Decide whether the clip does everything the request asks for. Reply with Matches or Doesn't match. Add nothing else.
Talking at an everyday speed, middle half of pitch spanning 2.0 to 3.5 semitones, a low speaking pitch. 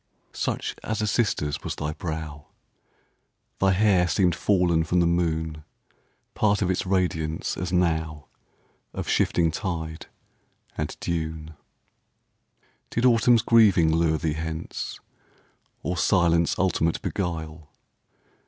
Doesn't match